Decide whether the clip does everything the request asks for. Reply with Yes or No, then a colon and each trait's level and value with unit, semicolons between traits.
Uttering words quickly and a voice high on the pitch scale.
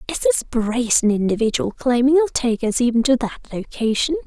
No: average, 170 wpm; very high, 250 Hz